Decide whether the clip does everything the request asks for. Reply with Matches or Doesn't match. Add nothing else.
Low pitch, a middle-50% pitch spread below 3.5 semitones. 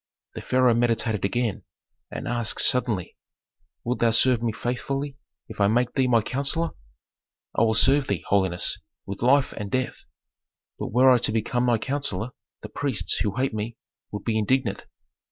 Matches